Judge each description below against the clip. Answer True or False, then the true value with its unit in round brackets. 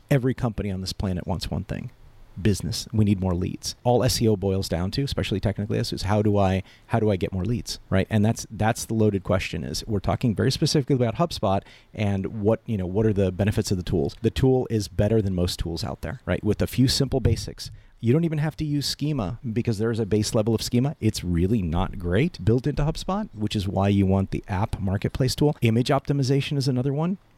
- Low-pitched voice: True (110 Hz)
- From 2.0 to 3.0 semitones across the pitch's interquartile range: False (4.3 semitones)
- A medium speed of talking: False (230 wpm)